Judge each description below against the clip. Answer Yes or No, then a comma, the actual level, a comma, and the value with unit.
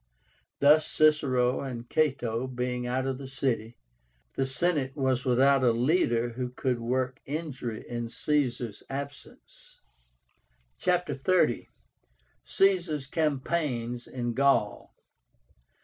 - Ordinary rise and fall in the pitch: Yes, average, 3.1 semitones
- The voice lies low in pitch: Yes, low, 130 Hz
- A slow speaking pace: Yes, slow, 105 wpm